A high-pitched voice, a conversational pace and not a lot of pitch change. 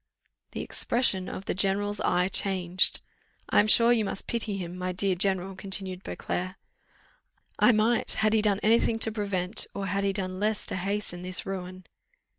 Yes: high, 195 Hz; average, 180 wpm; narrow, 2.3 semitones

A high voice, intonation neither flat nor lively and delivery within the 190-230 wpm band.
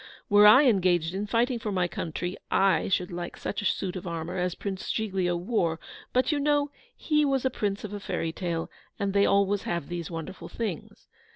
Yes: high, 195 Hz; average, 3.8 semitones; average, 200 wpm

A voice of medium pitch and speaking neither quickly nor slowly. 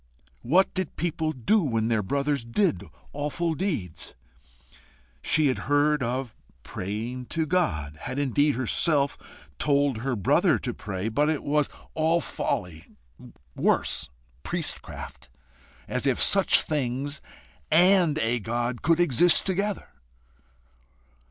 No: medium, 145 Hz; slow, 120 wpm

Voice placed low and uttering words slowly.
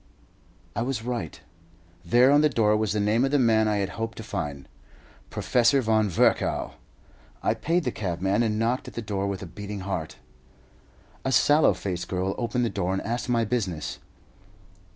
No: low, 110 Hz; average, 180 wpm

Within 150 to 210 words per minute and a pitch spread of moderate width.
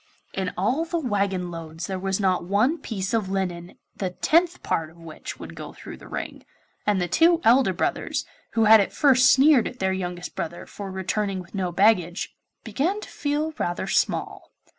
No: average, 185 wpm; wide, 5.9 semitones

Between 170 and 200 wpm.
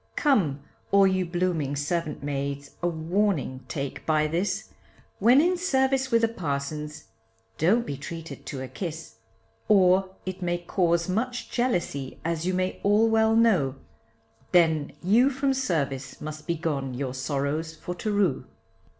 No: average, 150 wpm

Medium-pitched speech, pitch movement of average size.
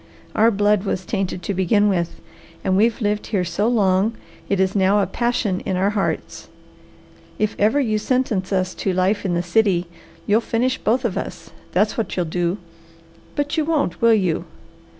No: high, 205 Hz; average, 3.2 semitones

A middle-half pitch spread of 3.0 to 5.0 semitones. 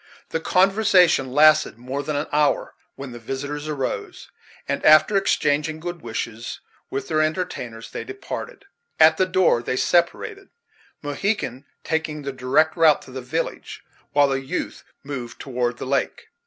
Yes: average, 3.7 semitones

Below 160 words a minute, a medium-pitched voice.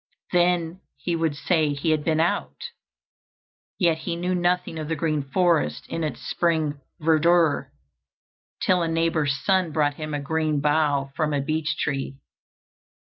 Yes: average, 150 wpm; medium, 160 Hz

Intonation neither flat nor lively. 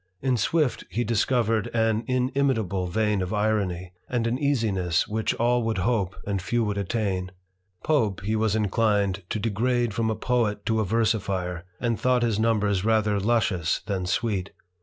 Yes: average, 3.0 semitones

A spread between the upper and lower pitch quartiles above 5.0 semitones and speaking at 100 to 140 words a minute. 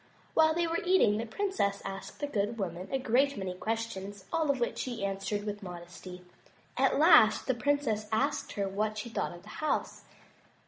No: wide, 5.6 semitones; average, 185 wpm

